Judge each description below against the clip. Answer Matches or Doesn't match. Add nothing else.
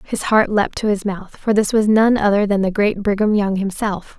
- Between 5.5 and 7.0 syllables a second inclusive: Doesn't match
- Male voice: Doesn't match